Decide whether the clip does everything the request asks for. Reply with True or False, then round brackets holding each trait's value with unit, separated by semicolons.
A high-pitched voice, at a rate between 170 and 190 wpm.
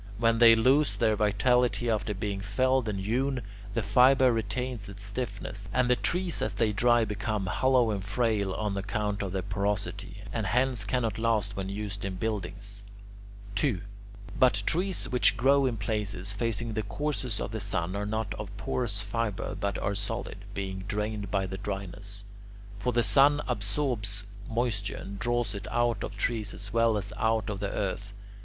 False (105 Hz; 175 wpm)